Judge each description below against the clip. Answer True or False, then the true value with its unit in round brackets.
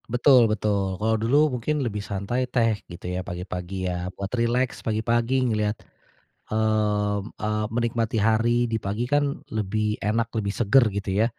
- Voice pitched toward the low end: True (110 Hz)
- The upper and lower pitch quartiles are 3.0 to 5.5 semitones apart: False (2.6 semitones)